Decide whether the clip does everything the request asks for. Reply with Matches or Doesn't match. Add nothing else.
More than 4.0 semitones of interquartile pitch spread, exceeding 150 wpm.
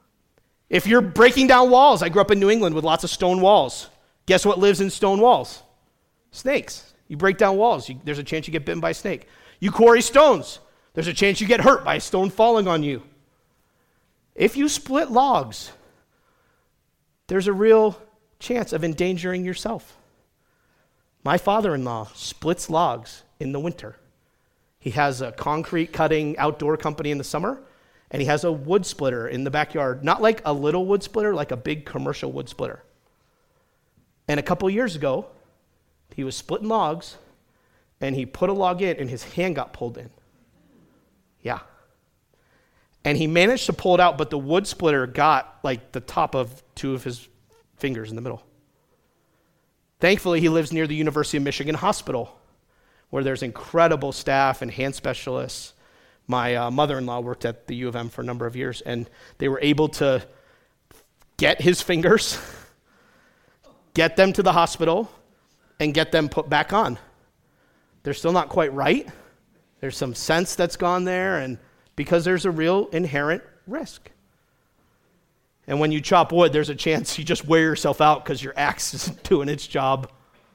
Matches